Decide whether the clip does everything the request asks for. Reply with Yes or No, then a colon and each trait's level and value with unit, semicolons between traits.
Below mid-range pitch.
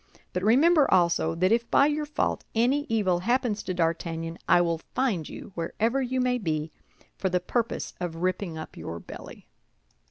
No: high, 190 Hz